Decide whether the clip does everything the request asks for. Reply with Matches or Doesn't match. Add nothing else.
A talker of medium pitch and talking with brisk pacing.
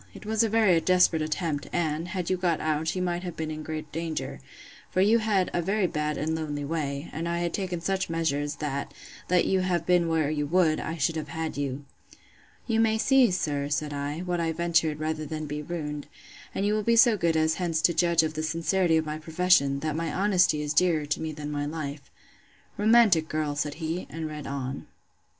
Matches